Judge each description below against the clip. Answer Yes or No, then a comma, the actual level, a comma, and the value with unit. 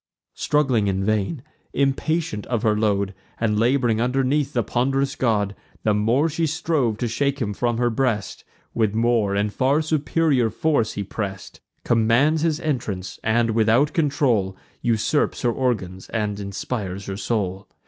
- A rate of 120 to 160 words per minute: Yes, average, 150 wpm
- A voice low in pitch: Yes, low, 115 Hz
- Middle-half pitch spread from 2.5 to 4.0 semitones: No, average, 4.7 semitones